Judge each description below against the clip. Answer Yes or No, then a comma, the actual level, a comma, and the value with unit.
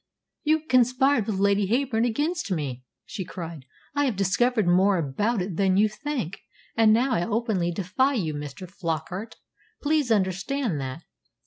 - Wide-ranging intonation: Yes, wide, 6.0 semitones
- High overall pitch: Yes, high, 205 Hz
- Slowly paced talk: No, average, 150 wpm